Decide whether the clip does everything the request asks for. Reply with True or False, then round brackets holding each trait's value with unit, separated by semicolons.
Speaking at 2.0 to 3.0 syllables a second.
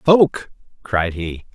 True (2.8 syllables/s)